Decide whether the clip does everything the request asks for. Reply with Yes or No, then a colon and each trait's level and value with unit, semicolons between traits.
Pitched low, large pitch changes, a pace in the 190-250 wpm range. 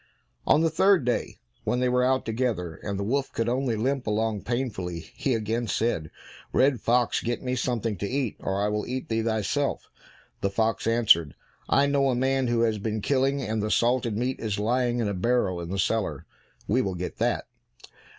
No: low, 115 Hz; average, 3.5 semitones; average, 200 wpm